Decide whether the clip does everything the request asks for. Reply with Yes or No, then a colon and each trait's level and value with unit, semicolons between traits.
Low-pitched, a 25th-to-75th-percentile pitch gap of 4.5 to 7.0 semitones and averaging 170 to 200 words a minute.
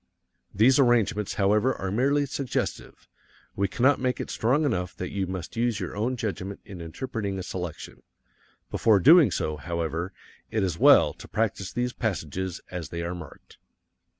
No: low, 100 Hz; average, 5.2 semitones; average, 160 wpm